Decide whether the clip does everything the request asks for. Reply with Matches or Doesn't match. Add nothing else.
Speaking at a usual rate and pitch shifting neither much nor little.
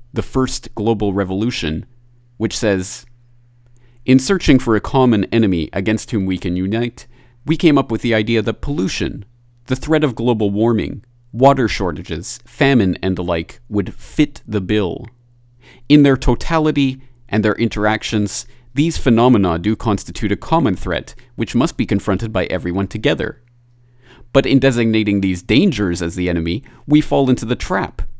Matches